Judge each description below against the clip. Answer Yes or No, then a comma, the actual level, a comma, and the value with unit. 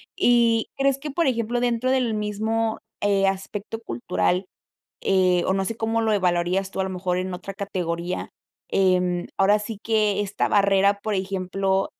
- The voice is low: No, high, 200 Hz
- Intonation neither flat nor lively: Yes, average, 3.1 semitones